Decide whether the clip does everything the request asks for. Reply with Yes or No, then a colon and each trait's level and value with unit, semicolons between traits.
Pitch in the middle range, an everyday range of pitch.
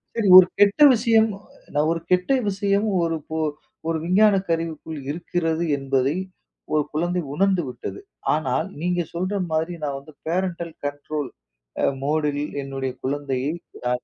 Yes: medium, 165 Hz; average, 3.8 semitones